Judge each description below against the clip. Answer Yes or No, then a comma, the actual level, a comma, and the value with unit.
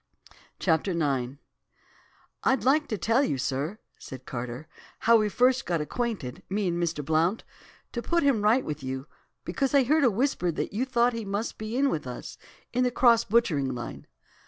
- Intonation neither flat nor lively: No, wide, 8.6 semitones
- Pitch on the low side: No, high, 210 Hz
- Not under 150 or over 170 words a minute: No, average, 180 wpm